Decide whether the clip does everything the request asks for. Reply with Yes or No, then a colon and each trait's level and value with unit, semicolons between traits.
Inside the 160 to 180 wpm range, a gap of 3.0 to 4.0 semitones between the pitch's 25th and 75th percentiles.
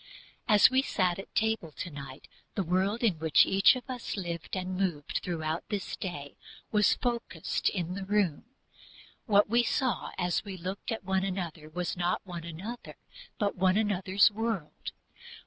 Yes: average, 165 wpm; average, 3.4 semitones